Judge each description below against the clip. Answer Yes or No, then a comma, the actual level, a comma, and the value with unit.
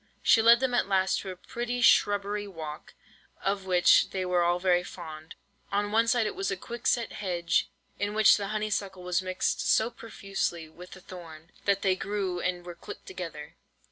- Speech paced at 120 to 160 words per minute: No, average, 195 wpm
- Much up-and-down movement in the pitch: No, average, 2.8 semitones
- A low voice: No, high, 190 Hz